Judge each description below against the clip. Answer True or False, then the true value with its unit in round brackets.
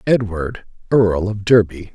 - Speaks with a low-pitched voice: True (100 Hz)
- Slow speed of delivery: True (125 wpm)